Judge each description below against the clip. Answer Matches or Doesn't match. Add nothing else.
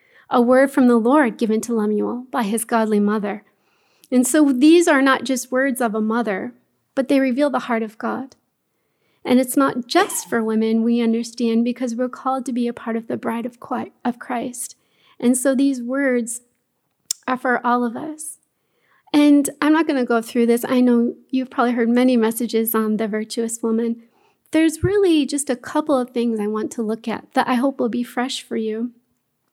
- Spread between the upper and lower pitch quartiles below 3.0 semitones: Matches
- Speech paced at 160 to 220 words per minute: Matches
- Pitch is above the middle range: Matches